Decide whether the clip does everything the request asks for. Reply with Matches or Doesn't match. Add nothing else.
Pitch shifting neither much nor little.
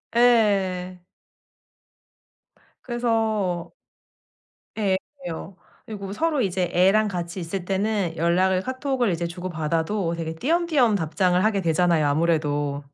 Matches